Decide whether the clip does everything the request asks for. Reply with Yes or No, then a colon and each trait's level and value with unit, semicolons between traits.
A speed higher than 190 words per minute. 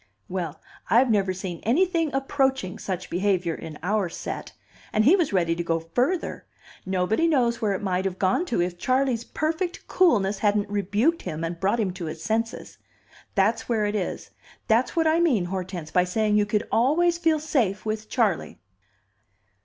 No: average, 175 wpm